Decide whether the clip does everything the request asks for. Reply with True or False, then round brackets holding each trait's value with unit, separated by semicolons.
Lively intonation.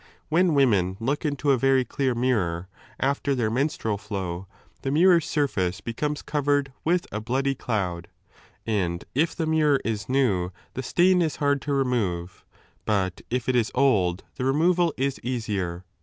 True (6.1 semitones)